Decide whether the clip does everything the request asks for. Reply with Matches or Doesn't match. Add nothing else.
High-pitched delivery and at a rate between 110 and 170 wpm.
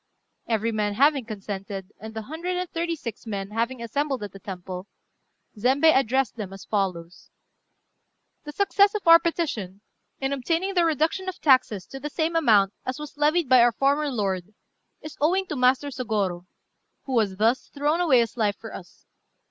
Doesn't match